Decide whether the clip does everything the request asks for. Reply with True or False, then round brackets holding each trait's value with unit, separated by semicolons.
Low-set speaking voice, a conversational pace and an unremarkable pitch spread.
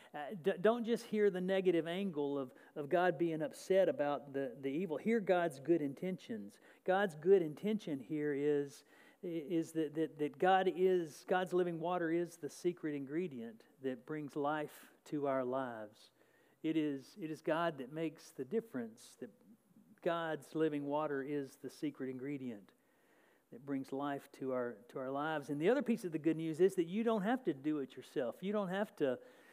False (160 Hz; 185 wpm; 4.7 semitones)